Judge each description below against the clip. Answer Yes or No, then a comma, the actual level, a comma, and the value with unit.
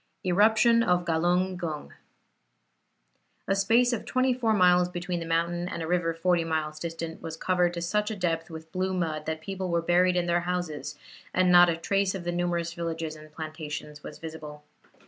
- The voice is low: No, medium, 175 Hz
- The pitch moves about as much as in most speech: No, narrow, 2.1 semitones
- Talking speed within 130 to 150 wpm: No, average, 185 wpm